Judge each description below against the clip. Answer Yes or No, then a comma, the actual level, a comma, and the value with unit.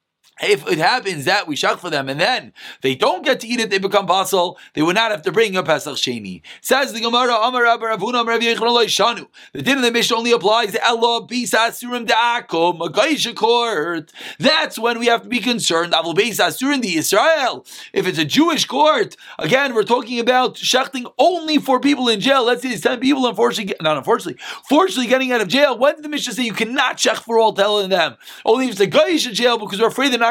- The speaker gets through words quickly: Yes, fast, 215 wpm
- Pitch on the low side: No, high, 235 Hz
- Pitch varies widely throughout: No, average, 3.8 semitones